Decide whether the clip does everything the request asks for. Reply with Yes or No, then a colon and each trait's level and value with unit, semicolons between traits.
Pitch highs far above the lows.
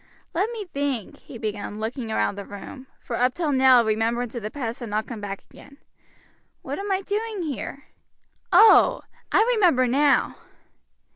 Yes: wide, 7.9 semitones